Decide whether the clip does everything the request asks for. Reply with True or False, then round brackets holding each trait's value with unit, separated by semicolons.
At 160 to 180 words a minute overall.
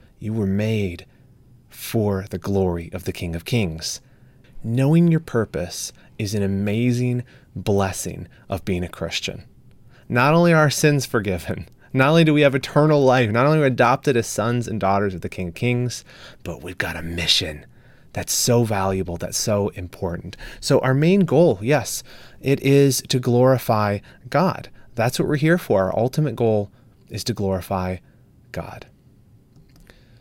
True (165 wpm)